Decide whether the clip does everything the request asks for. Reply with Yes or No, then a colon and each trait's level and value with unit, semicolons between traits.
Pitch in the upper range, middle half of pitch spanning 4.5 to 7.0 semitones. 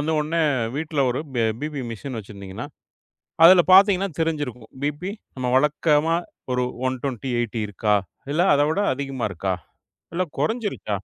No: medium, 145 Hz; average, 5.2 semitones